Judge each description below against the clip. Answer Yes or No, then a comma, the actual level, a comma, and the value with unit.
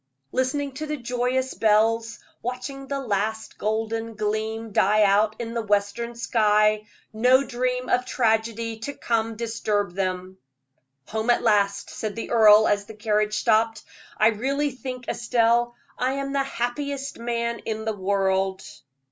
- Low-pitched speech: No, high, 225 Hz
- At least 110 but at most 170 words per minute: Yes, average, 145 wpm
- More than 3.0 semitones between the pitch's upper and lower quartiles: No, average, 2.7 semitones